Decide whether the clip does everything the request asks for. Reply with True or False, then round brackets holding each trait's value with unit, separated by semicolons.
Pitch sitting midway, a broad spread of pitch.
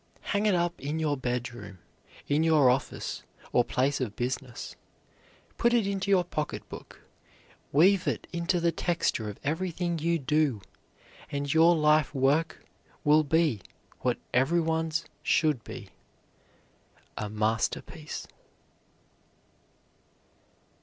False (155 Hz; 4.5 semitones)